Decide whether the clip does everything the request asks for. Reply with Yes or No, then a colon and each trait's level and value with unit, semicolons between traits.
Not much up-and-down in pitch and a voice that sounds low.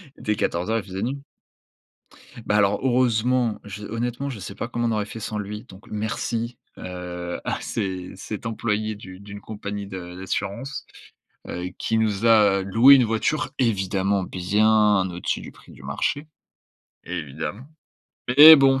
No: average, 3.3 semitones; low, 105 Hz